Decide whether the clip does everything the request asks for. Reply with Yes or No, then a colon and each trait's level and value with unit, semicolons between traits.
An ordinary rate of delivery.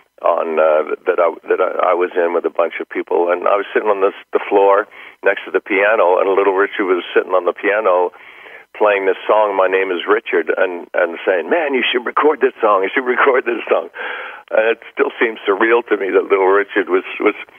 No: fast, 230 wpm